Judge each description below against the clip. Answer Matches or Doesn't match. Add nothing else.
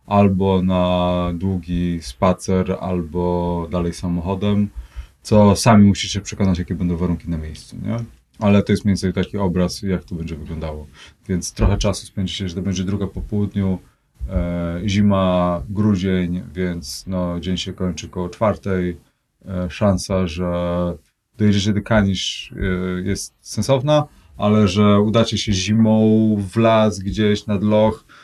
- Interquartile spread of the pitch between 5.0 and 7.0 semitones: Doesn't match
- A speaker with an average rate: Matches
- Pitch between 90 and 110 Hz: Matches